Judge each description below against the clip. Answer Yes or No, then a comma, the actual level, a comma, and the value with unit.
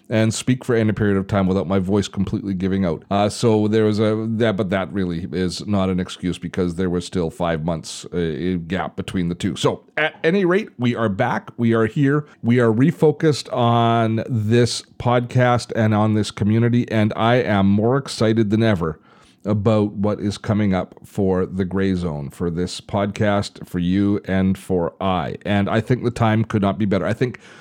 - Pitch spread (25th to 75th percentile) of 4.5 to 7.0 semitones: No, average, 3.3 semitones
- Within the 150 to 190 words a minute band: No, average, 200 wpm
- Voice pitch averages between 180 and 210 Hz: No, low, 105 Hz